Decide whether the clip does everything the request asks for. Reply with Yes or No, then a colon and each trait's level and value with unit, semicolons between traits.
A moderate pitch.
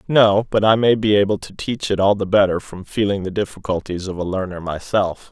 No: low, 100 Hz